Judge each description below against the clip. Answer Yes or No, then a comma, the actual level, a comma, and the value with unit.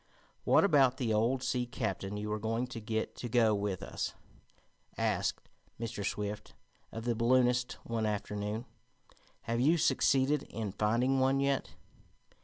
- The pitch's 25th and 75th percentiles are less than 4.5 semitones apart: Yes, average, 3.2 semitones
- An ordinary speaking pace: Yes, average, 145 wpm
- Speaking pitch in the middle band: No, low, 115 Hz